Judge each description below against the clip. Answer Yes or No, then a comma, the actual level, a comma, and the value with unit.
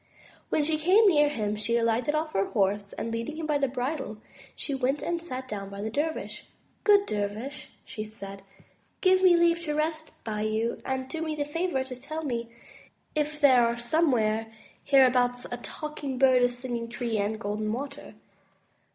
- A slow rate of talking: No, average, 185 wpm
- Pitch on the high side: Yes, very high, 260 Hz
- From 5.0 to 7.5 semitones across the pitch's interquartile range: Yes, average, 5.3 semitones